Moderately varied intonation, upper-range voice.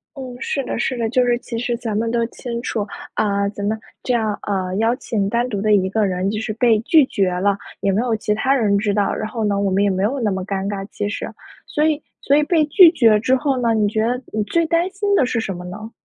Yes: average, 3.7 semitones; high, 220 Hz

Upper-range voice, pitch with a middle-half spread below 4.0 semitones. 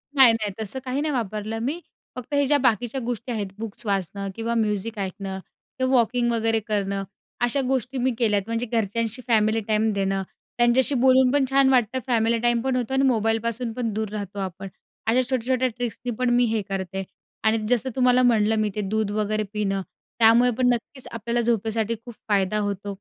Yes: high, 225 Hz; average, 2.9 semitones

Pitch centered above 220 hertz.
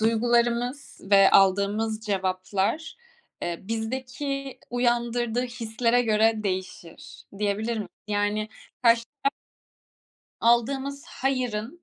Yes: high, 230 Hz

